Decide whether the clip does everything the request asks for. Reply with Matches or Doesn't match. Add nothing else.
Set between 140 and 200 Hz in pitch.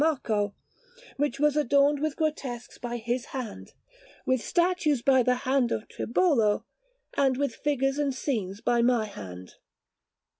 Doesn't match